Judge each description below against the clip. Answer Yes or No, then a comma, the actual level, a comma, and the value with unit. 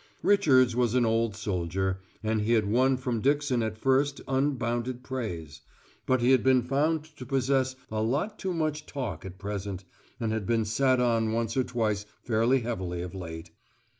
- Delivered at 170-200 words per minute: Yes, average, 175 wpm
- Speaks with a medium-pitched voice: No, low, 120 Hz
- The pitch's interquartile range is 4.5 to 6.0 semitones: No, average, 3.7 semitones